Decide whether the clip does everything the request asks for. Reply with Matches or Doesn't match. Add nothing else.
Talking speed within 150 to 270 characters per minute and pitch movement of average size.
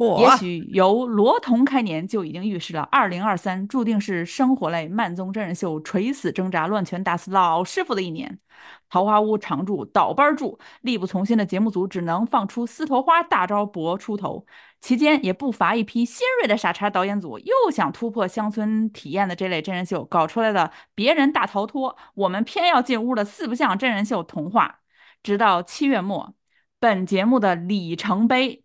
Doesn't match